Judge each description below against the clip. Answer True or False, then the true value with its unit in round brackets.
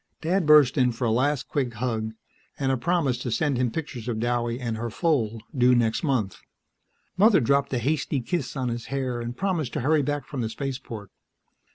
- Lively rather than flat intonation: False (3.7 semitones)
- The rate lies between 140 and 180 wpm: False (200 wpm)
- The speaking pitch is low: True (125 Hz)